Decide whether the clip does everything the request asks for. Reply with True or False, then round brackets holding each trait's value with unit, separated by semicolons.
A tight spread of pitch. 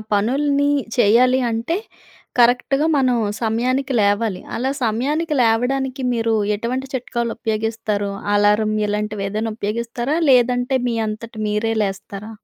False (3.2 semitones)